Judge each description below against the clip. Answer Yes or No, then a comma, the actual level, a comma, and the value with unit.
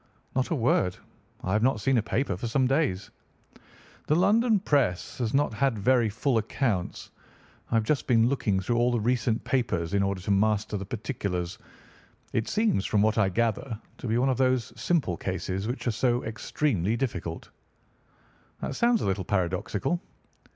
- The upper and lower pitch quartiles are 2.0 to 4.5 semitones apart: No, average, 5.0 semitones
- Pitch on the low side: Yes, low, 115 Hz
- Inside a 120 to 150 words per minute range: No, average, 175 wpm